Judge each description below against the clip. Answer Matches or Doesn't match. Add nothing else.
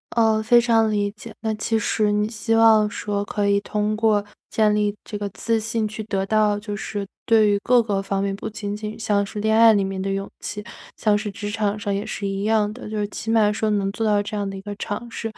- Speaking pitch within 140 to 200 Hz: Doesn't match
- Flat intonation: Matches